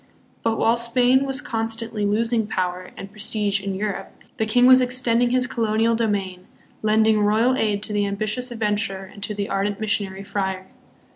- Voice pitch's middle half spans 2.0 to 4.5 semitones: Yes, narrow, 2.5 semitones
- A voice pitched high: Yes, high, 215 Hz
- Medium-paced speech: Yes, average, 170 wpm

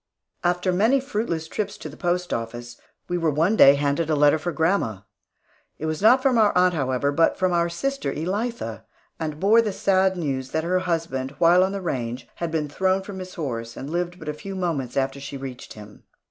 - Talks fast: Yes, fast, 210 wpm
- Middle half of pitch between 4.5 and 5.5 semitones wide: Yes, average, 4.9 semitones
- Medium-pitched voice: Yes, medium, 165 Hz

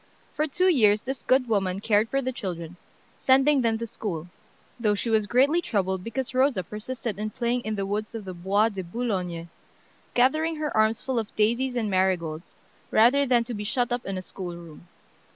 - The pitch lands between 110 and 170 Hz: No, high, 220 Hz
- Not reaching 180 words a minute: No, average, 190 wpm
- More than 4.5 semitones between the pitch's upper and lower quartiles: Yes, average, 4.9 semitones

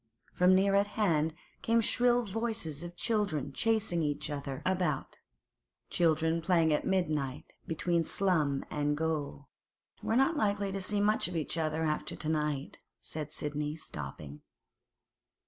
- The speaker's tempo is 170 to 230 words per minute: No, slow, 135 wpm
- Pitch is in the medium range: Yes, medium, 160 Hz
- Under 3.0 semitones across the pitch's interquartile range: No, average, 4.8 semitones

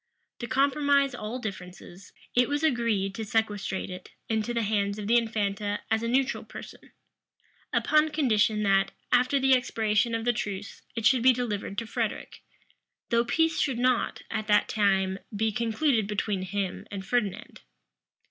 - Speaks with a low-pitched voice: No, high, 220 Hz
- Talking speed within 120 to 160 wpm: Yes, average, 155 wpm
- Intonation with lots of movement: No, average, 3.5 semitones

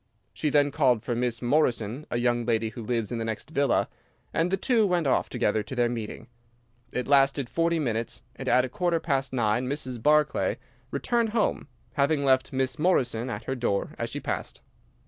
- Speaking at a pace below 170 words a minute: No, average, 190 wpm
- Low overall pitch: Yes, low, 130 Hz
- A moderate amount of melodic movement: Yes, average, 4.1 semitones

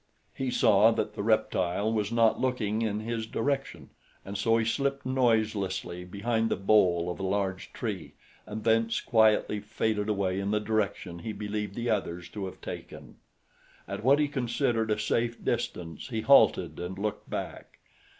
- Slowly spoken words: No, average, 165 wpm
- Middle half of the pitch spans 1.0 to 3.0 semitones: Yes, narrow, 2.6 semitones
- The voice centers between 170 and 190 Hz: No, low, 110 Hz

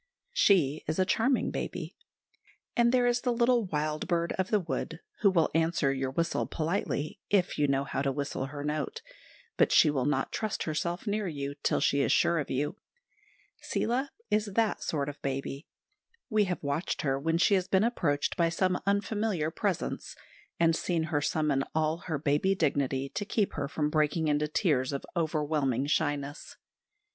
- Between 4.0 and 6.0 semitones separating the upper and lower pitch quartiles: Yes, average, 5.1 semitones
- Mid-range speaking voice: Yes, medium, 160 Hz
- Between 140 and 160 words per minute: No, average, 175 wpm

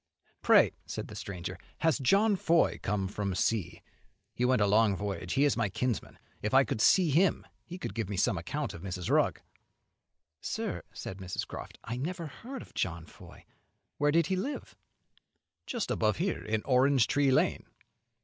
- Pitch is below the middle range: Yes, low, 125 Hz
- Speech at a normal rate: Yes, average, 180 wpm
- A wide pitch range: Yes, wide, 8.4 semitones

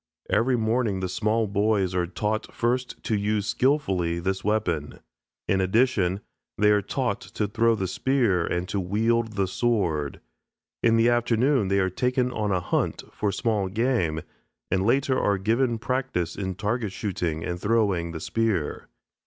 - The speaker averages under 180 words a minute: Yes, average, 160 wpm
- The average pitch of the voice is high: No, low, 105 Hz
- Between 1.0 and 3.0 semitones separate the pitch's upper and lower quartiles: No, average, 3.9 semitones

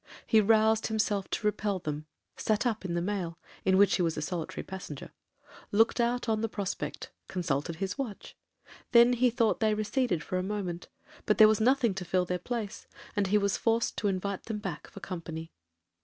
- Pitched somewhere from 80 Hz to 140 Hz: No, high, 205 Hz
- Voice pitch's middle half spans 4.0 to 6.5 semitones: No, average, 3.5 semitones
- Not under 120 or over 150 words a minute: No, average, 175 wpm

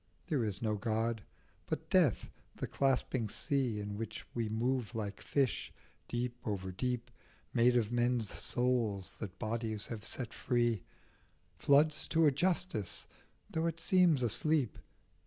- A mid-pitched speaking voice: No, low, 120 Hz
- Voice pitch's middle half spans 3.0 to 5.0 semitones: Yes, average, 3.5 semitones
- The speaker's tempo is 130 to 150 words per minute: Yes, average, 140 wpm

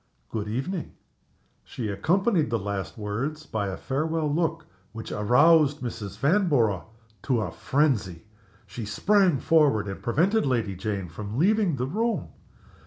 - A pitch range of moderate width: No, wide, 7.5 semitones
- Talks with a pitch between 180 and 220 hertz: No, low, 130 Hz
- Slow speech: Yes, slow, 130 wpm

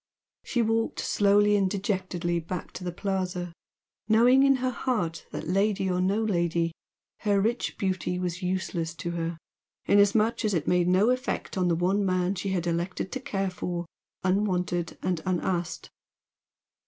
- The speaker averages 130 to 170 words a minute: Yes, average, 155 wpm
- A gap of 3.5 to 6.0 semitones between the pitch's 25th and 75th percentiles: No, average, 2.7 semitones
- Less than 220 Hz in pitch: Yes, medium, 185 Hz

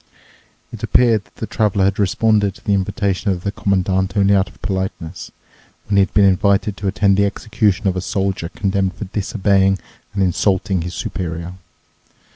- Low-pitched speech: Yes, low, 100 Hz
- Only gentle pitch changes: Yes, narrow, 1.4 semitones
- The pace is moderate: Yes, average, 175 wpm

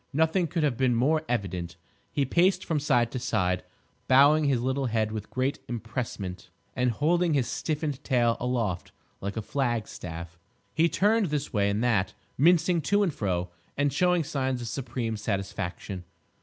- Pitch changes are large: Yes, wide, 5.9 semitones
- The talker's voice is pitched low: Yes, low, 125 Hz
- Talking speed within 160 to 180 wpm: Yes, average, 165 wpm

